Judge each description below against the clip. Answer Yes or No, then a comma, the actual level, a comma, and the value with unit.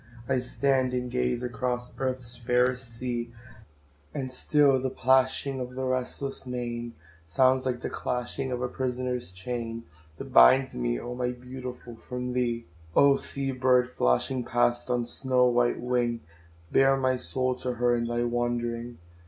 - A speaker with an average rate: Yes, average, 155 wpm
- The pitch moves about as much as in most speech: No, narrow, 1.3 semitones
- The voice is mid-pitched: No, low, 125 Hz